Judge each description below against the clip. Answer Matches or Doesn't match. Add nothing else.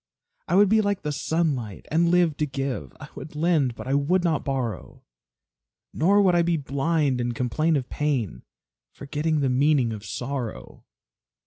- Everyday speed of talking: Matches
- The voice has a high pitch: Doesn't match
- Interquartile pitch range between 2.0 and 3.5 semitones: Doesn't match